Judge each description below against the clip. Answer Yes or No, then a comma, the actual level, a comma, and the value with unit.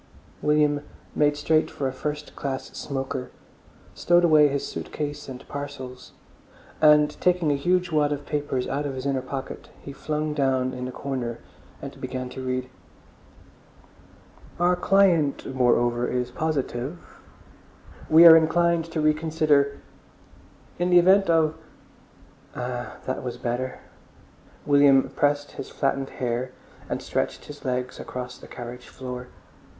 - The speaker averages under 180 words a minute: Yes, average, 140 wpm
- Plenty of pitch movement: No, average, 3.3 semitones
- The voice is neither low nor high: Yes, medium, 145 Hz